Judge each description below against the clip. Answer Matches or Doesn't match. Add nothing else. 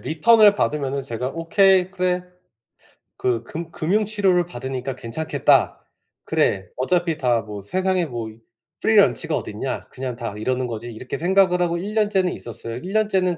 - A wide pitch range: Matches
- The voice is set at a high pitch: Doesn't match